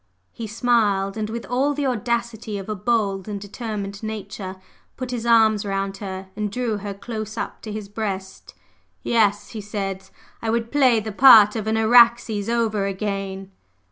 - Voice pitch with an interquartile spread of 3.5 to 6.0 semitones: No, average, 2.7 semitones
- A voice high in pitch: Yes, high, 215 Hz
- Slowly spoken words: No, average, 170 wpm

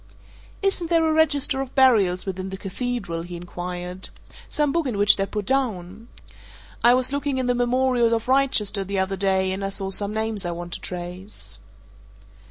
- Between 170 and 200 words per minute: Yes, average, 180 wpm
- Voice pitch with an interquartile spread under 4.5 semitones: No, wide, 5.5 semitones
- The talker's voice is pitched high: Yes, high, 210 Hz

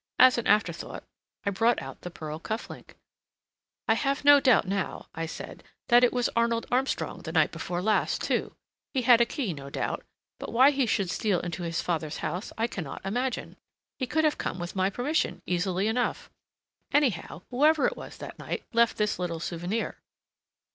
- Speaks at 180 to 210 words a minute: Yes, average, 190 wpm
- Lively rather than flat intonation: Yes, wide, 5.9 semitones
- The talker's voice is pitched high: Yes, high, 220 Hz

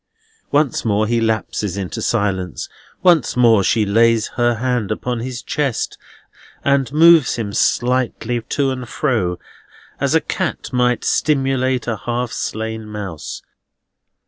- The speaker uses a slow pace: Yes, slow, 130 wpm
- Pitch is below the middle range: Yes, low, 120 Hz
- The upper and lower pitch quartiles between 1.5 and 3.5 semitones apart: Yes, average, 3.0 semitones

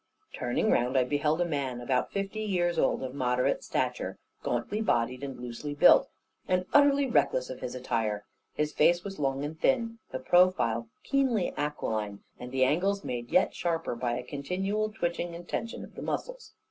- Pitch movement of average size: No, wide, 7.6 semitones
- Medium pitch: Yes, medium, 150 Hz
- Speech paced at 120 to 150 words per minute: No, average, 175 wpm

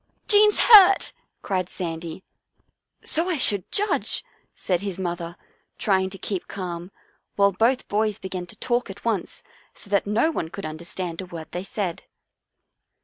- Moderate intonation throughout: Yes, average, 4.2 semitones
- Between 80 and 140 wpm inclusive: No, average, 160 wpm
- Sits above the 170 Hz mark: Yes, high, 190 Hz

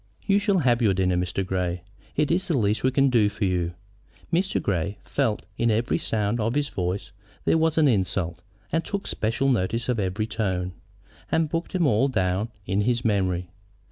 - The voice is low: Yes, low, 110 Hz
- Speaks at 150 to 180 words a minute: No, average, 195 wpm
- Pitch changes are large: Yes, wide, 6.6 semitones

